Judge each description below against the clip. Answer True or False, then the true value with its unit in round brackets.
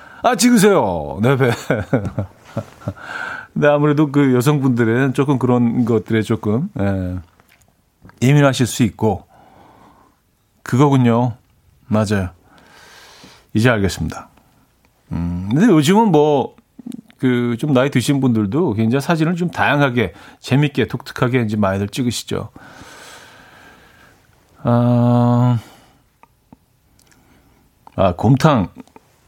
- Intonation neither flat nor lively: True (4.8 semitones)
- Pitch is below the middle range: True (125 Hz)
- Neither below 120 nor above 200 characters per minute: True (195 characters per minute)